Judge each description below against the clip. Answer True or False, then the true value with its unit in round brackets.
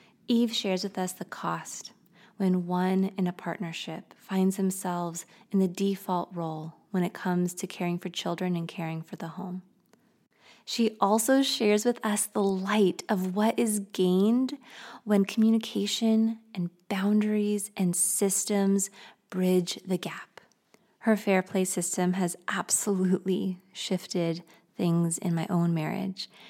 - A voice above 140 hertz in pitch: True (190 Hz)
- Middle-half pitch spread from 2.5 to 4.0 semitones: True (2.9 semitones)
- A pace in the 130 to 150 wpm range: True (140 wpm)